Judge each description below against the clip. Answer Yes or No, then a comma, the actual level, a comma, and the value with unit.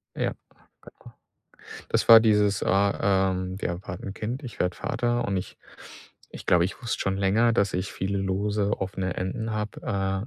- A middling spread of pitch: No, narrow, 2.3 semitones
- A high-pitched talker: No, low, 100 Hz